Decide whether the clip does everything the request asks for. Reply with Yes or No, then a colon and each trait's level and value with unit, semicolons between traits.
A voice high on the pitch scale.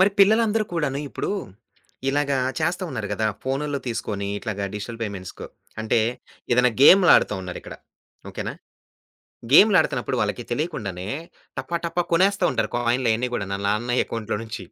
No: low, 125 Hz